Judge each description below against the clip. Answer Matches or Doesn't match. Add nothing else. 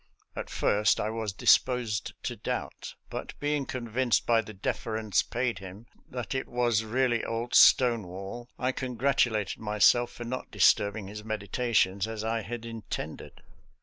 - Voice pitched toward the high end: Doesn't match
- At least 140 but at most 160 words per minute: Matches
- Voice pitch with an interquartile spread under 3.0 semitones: Matches